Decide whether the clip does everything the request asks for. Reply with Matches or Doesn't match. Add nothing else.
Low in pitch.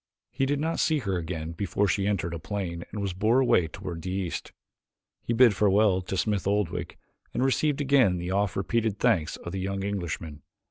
Matches